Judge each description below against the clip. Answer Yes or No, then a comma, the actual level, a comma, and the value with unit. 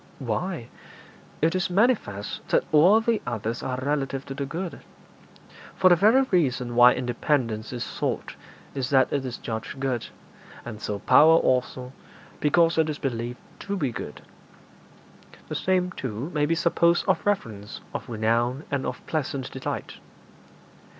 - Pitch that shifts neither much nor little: No, wide, 5.7 semitones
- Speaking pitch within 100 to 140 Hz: Yes, low, 135 Hz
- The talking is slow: No, average, 150 wpm